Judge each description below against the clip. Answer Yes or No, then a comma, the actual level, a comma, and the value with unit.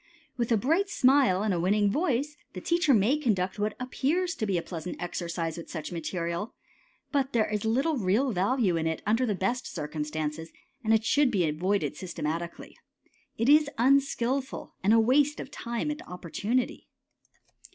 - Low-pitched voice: No, high, 215 Hz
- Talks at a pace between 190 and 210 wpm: No, average, 170 wpm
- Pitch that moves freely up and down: Yes, wide, 6.9 semitones